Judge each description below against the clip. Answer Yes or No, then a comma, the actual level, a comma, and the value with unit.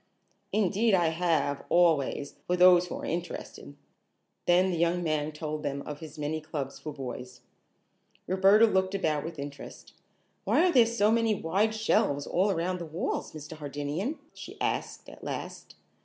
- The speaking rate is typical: Yes, average, 160 wpm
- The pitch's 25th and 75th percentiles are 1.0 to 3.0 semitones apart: No, average, 4.2 semitones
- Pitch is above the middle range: No, medium, 170 Hz